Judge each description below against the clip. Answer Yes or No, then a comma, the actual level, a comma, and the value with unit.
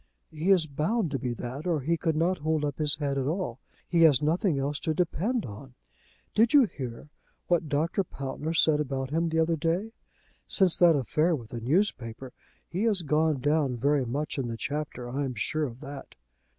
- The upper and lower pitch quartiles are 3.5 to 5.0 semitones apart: Yes, average, 3.8 semitones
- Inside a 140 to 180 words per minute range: No, average, 200 wpm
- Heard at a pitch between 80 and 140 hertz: No, medium, 150 Hz